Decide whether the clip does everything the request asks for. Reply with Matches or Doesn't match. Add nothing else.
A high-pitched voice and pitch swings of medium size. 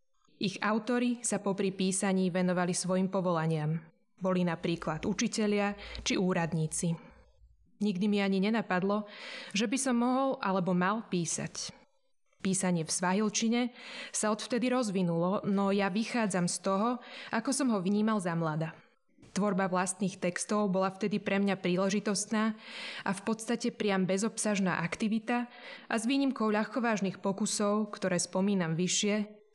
Matches